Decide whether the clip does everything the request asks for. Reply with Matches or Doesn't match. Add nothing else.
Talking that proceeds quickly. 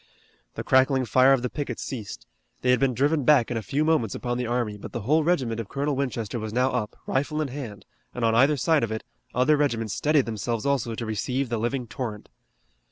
Matches